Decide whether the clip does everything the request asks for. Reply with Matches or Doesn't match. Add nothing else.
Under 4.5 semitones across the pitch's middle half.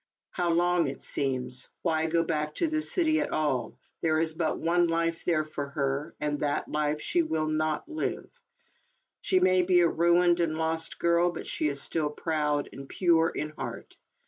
Matches